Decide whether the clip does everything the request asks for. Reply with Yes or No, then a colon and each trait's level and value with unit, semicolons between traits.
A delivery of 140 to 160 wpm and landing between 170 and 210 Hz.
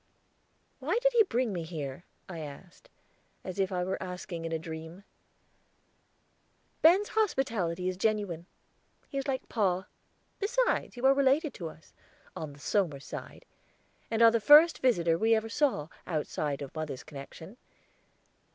Yes: average, 150 wpm; high, 190 Hz